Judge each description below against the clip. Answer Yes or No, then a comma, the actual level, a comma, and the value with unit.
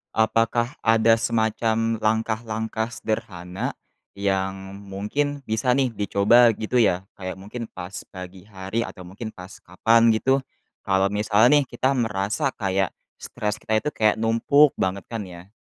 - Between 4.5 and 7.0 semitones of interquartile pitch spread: No, average, 3.0 semitones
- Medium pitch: No, low, 110 Hz